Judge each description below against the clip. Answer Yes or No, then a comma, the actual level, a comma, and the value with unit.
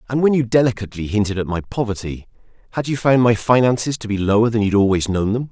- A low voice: Yes, low, 110 Hz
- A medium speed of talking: No, fast, 230 wpm